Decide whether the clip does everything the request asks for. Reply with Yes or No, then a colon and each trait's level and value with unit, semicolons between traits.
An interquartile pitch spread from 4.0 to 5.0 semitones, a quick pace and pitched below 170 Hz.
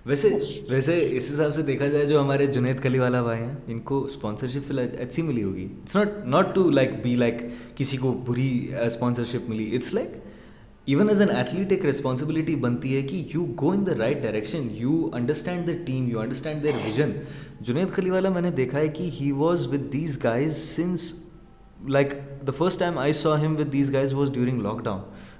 Yes: average, 4.4 semitones; fast, 200 wpm; medium, 140 Hz